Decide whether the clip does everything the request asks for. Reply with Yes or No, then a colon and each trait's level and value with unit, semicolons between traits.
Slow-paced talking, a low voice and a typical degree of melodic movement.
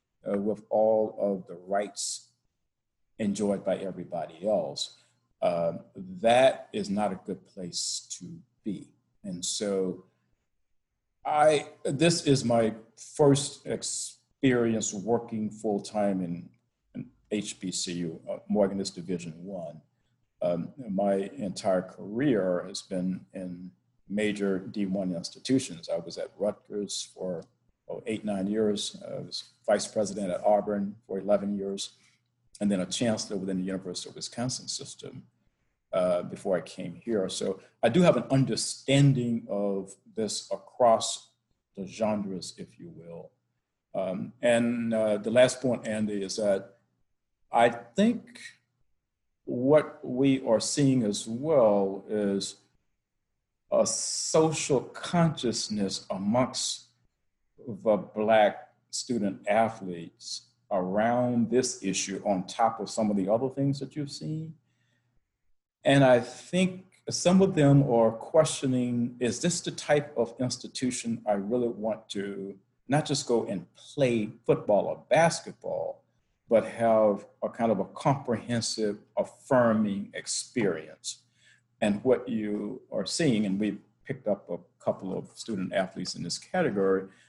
Yes: slow, 130 wpm; low, 110 Hz; average, 4.2 semitones